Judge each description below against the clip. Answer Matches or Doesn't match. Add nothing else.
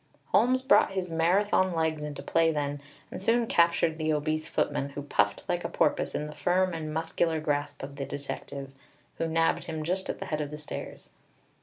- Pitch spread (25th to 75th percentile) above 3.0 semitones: Doesn't match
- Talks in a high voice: Doesn't match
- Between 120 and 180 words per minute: Doesn't match